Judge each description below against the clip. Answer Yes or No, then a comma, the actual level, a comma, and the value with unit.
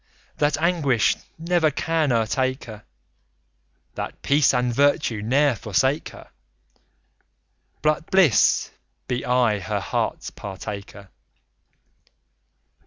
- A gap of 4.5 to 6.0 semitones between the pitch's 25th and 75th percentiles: Yes, wide, 5.4 semitones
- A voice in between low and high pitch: No, low, 130 Hz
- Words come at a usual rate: No, slow, 95 wpm